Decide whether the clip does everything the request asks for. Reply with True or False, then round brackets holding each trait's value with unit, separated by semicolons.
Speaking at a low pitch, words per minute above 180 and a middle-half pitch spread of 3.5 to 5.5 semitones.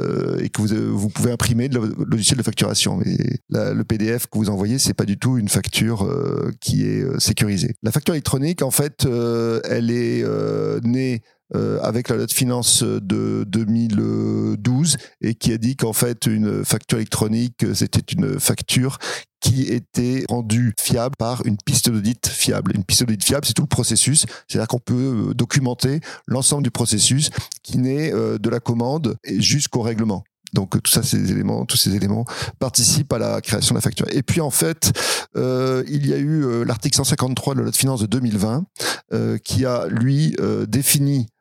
False (120 Hz; 190 wpm; 3.1 semitones)